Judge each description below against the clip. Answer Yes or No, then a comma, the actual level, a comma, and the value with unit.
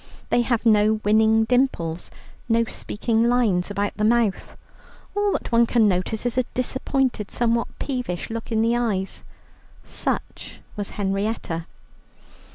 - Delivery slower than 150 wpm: Yes, slow, 135 wpm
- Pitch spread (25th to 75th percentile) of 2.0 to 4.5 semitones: Yes, average, 2.7 semitones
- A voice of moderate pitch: No, high, 225 Hz